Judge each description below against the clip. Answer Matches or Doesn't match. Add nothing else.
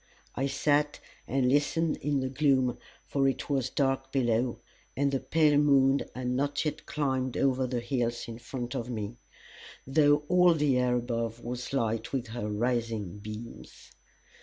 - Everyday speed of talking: Matches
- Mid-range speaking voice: Doesn't match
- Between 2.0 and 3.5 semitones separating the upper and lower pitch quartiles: Matches